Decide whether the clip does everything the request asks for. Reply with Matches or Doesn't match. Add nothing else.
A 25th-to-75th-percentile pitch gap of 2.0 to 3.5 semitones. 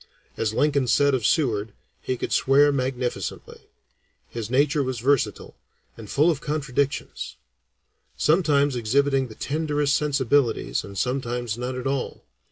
Matches